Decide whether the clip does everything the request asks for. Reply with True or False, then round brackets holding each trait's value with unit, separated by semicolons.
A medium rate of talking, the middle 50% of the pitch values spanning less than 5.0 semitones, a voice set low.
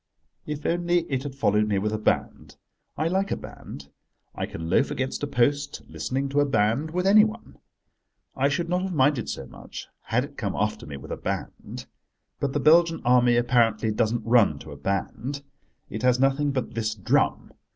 False (190 wpm; 5.3 semitones; 130 Hz)